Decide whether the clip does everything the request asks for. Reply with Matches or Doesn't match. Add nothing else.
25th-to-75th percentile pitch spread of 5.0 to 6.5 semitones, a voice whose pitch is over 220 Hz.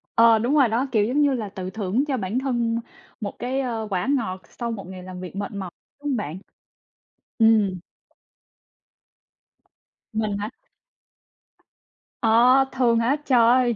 Doesn't match